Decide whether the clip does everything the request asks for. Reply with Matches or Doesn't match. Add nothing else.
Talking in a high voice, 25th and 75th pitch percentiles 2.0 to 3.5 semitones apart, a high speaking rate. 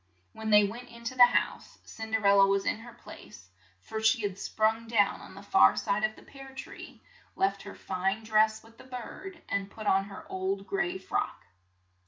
Matches